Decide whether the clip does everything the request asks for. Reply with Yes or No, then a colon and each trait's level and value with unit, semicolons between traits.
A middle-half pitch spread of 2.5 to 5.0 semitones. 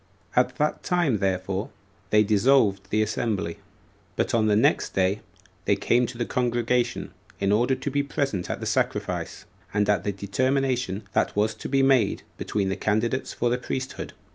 Yes: average, 4.2 semitones